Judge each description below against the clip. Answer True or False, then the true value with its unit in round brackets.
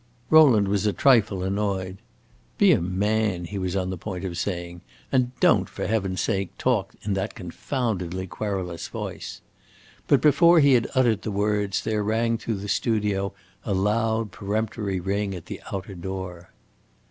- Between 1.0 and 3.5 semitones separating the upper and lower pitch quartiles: True (2.9 semitones)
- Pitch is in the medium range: False (100 Hz)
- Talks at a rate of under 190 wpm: True (160 wpm)